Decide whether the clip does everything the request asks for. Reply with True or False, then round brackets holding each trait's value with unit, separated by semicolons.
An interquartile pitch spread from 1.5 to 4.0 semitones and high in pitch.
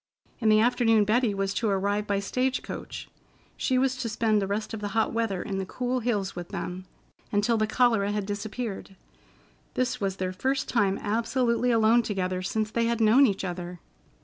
True (3.0 semitones; 215 Hz)